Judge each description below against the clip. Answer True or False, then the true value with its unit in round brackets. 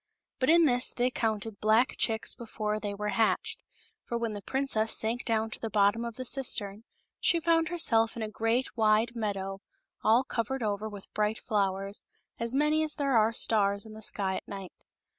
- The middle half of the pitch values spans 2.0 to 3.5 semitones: True (2.8 semitones)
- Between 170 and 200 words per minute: True (190 wpm)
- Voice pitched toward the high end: True (225 Hz)